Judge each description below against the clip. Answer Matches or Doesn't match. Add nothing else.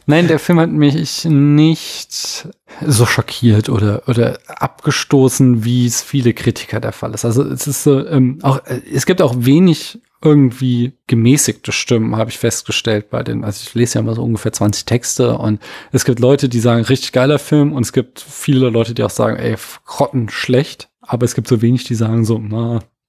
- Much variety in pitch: Doesn't match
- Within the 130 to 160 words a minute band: Doesn't match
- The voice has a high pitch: Doesn't match